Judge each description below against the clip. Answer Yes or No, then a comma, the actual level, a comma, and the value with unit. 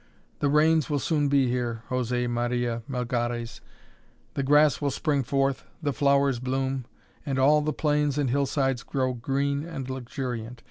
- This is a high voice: No, low, 135 Hz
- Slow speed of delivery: No, average, 150 wpm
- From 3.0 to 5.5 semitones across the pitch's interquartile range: No, narrow, 2.6 semitones